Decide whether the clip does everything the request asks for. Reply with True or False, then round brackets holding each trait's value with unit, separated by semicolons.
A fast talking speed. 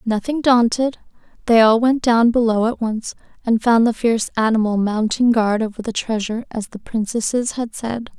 False (175 wpm)